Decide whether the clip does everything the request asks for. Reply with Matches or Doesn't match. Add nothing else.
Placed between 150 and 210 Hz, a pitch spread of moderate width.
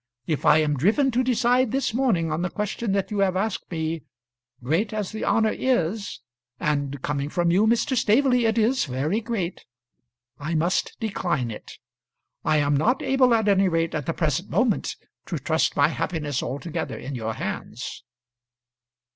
Doesn't match